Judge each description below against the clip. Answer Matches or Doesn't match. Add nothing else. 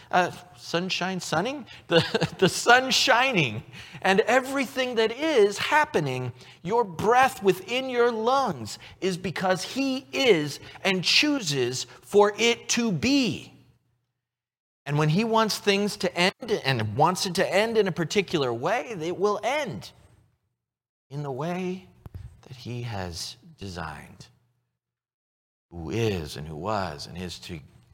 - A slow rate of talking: Matches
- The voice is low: Doesn't match